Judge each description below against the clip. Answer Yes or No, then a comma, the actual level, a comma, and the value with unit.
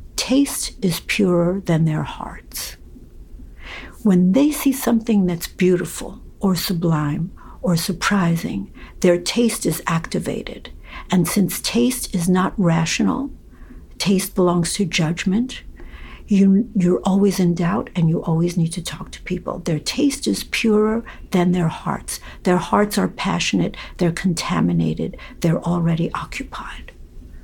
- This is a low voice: No, medium, 180 Hz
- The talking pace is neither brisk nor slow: No, slow, 130 wpm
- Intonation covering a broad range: No, average, 3.2 semitones